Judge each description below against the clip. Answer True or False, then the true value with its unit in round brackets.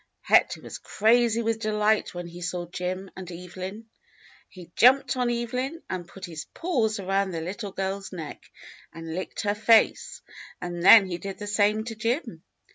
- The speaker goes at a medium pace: True (170 wpm)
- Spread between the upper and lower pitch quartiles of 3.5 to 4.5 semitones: True (3.8 semitones)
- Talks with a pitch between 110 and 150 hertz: False (200 Hz)